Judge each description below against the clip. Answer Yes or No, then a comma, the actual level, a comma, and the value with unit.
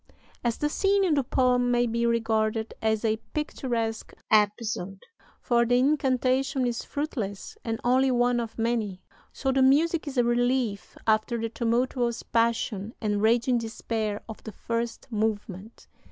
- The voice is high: Yes, high, 235 Hz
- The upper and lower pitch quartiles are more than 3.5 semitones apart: No, narrow, 2.5 semitones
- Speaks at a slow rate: No, average, 150 wpm